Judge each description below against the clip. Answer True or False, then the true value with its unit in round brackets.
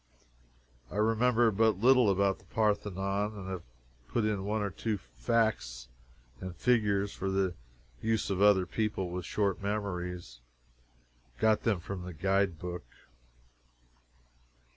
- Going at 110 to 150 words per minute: True (135 wpm)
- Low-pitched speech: True (100 Hz)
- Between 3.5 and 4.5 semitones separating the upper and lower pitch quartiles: False (2.9 semitones)